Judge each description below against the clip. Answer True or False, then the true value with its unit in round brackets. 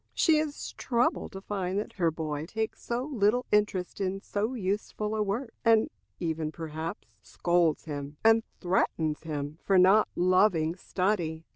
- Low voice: False (190 Hz)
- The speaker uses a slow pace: False (150 wpm)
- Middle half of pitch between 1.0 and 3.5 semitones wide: False (4.8 semitones)